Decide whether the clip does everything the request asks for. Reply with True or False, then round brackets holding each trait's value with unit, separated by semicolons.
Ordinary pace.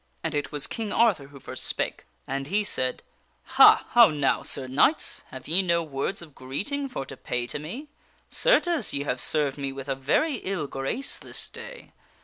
True (195 wpm)